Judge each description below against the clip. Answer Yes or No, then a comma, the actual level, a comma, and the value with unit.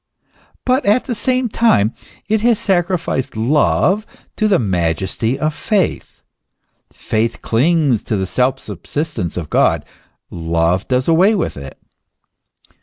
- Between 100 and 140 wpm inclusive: Yes, slow, 135 wpm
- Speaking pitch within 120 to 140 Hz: Yes, low, 135 Hz